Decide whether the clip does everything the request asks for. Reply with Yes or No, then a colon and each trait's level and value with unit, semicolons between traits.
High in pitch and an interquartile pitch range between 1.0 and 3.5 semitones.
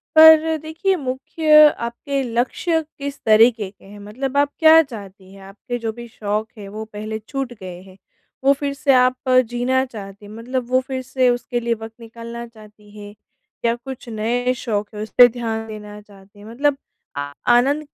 No: high, 235 Hz; average, 4.1 semitones